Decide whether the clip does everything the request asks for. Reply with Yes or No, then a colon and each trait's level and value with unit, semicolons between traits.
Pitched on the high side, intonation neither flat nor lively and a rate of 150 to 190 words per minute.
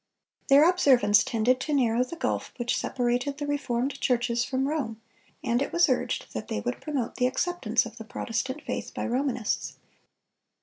Yes: very high, 250 Hz; average, 3.2 semitones; average, 170 wpm